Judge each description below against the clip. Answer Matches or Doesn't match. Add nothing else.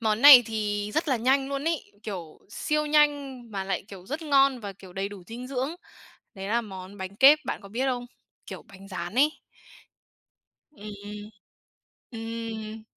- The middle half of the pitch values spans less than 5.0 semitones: Doesn't match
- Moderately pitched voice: Doesn't match